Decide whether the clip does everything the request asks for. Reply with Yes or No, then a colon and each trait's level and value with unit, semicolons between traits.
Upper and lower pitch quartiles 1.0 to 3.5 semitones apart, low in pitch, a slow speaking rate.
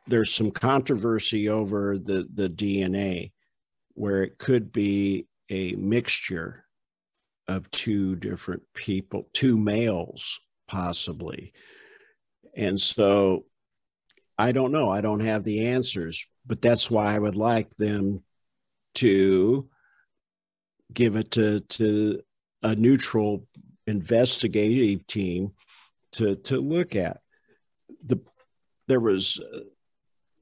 Yes: average, 3.1 semitones; low, 105 Hz; slow, 105 wpm